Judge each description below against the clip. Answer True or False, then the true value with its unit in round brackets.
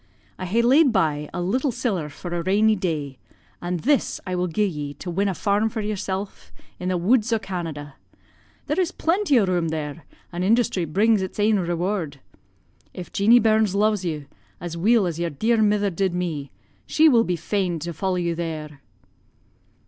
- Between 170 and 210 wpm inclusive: True (185 wpm)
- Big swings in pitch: False (4.3 semitones)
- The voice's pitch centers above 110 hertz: True (185 Hz)